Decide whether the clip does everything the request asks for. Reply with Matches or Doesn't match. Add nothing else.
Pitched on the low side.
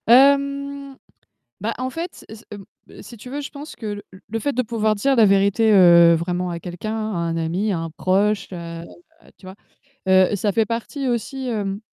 Doesn't match